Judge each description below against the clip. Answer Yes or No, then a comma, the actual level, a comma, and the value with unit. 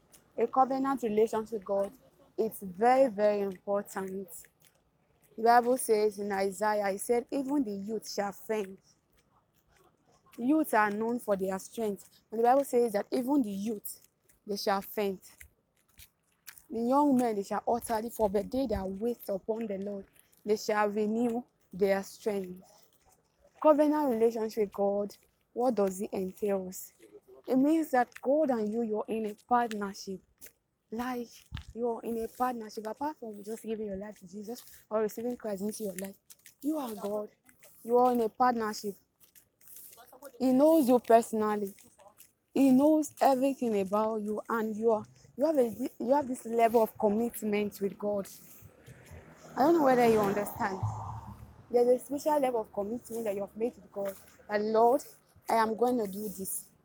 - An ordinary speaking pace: Yes, average, 160 wpm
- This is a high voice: Yes, high, 220 Hz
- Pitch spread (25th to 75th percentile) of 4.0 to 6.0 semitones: No, average, 3.2 semitones